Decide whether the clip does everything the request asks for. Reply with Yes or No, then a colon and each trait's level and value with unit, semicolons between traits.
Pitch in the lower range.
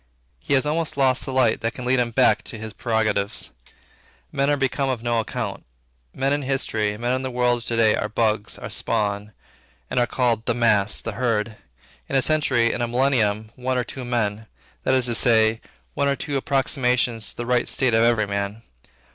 Yes: low, 120 Hz